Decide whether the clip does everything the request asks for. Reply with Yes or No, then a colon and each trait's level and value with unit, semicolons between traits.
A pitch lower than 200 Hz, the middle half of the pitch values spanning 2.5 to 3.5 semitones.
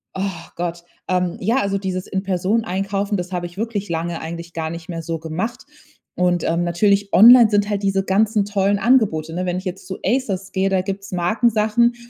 Yes: high, 190 Hz; average, 2.8 semitones